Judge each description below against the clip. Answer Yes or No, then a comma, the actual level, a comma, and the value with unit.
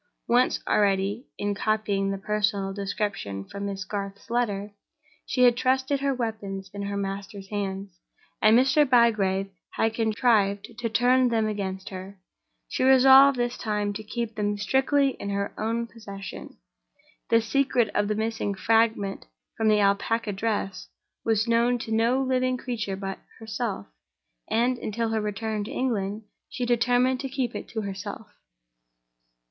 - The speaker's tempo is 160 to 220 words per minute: No, average, 150 wpm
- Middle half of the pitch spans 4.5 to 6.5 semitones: No, average, 3.3 semitones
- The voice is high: Yes, high, 215 Hz